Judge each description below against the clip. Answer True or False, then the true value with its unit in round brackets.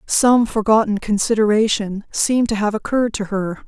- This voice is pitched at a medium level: False (215 Hz)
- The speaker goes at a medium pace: True (145 wpm)